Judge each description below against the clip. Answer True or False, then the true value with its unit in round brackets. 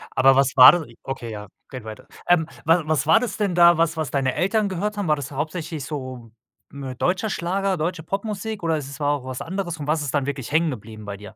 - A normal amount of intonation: True (5.0 semitones)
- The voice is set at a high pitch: False (155 Hz)